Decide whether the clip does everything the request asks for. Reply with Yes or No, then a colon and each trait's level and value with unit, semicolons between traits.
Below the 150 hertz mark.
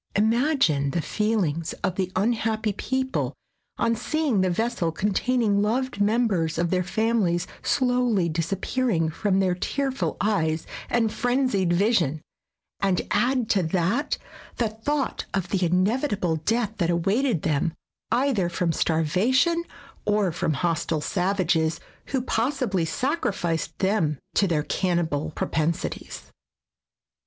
No: high, 195 Hz